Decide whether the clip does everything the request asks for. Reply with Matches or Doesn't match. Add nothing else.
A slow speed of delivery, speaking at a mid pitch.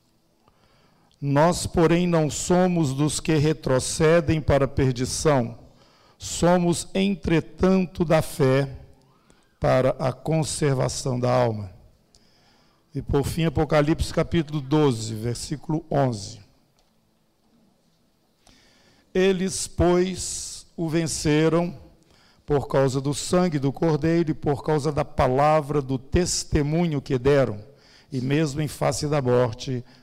Matches